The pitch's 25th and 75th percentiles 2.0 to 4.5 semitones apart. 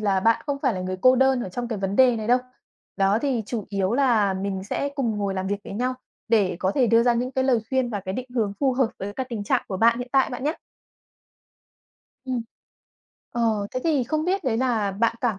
Yes: average, 4.2 semitones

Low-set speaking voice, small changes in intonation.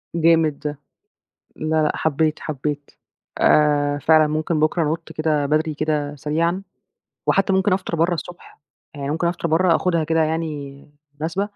No: medium, 155 Hz; narrow, 1.9 semitones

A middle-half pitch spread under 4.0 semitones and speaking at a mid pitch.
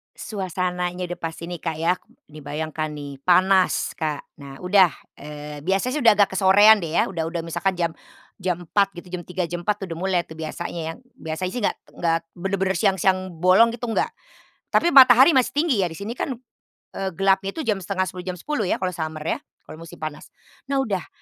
Yes: average, 3.1 semitones; medium, 180 Hz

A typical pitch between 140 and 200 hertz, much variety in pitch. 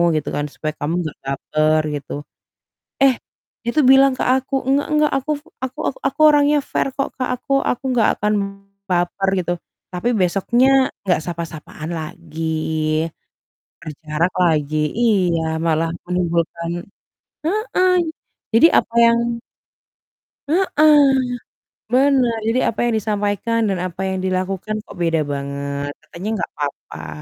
Yes: high, 190 Hz; wide, 7.5 semitones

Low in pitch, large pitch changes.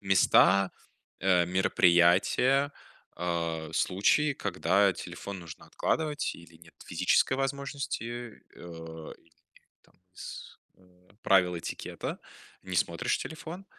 Yes: very low, 95 Hz; wide, 7.7 semitones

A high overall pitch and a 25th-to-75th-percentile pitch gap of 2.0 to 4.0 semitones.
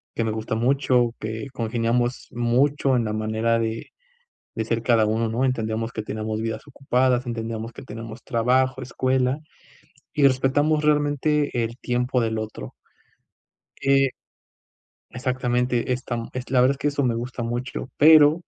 No: low, 125 Hz; narrow, 2.5 semitones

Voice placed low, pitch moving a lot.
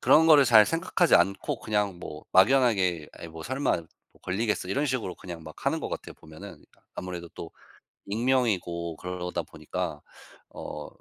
Yes: very low, 95 Hz; wide, 6.4 semitones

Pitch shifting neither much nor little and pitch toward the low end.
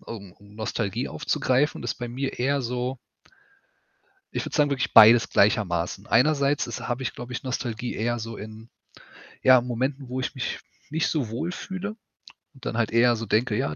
Yes: average, 3.1 semitones; low, 120 Hz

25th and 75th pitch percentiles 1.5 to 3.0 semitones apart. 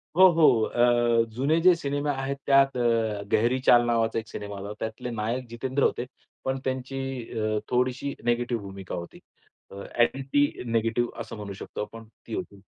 No: average, 3.4 semitones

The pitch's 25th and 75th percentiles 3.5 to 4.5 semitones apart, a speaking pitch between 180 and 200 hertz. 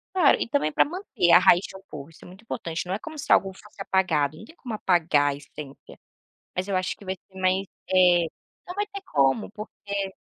Yes: average, 4.0 semitones; high, 190 Hz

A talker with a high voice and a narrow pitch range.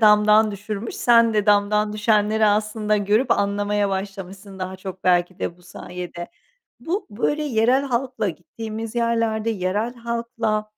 Yes: high, 210 Hz; narrow, 2.3 semitones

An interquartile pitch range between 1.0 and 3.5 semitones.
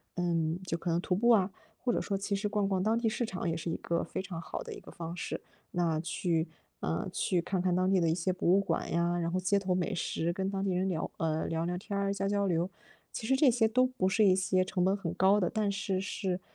Yes: narrow, 2.6 semitones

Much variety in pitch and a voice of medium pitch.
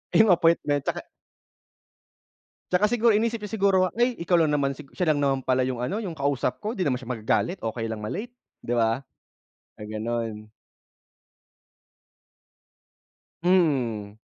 Yes: wide, 7.9 semitones; medium, 145 Hz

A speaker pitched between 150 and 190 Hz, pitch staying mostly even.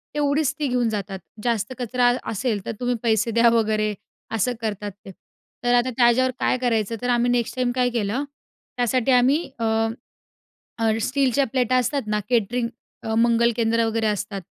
No: high, 235 Hz; narrow, 2.1 semitones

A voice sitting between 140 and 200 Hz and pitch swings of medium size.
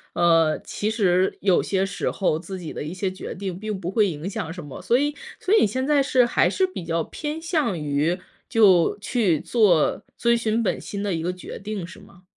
Yes: high, 195 Hz; average, 4.9 semitones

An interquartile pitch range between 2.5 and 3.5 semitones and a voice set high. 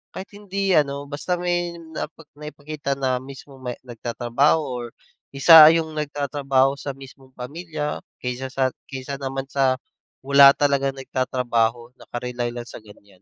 No: average, 3.0 semitones; low, 135 Hz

